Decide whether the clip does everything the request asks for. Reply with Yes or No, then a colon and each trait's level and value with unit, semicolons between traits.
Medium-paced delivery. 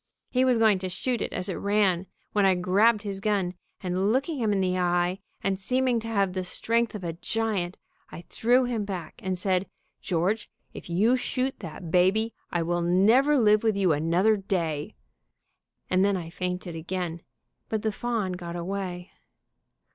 Yes: average, 175 wpm